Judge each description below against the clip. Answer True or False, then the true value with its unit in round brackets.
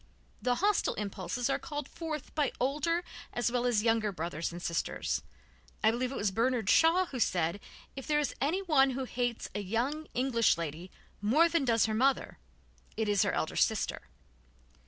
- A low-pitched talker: False (245 Hz)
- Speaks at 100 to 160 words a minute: False (175 wpm)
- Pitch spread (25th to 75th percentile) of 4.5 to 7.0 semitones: True (5.4 semitones)